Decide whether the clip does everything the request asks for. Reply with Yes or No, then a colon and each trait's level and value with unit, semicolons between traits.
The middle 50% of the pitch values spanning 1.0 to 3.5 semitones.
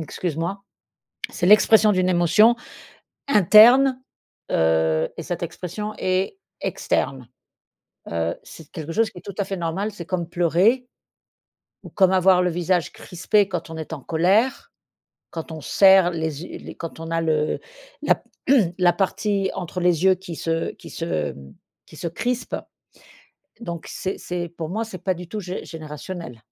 Yes: average, 3.2 semitones